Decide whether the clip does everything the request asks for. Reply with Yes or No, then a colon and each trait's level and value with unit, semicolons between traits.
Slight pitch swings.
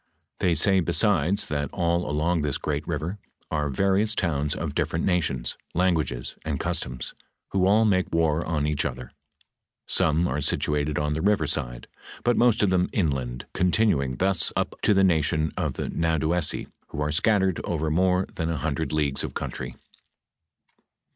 No: average, 4.0 semitones